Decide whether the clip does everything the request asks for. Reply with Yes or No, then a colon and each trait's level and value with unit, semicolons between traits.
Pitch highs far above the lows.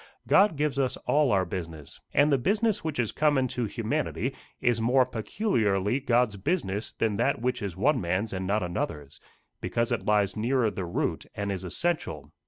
Yes: wide, 5.9 semitones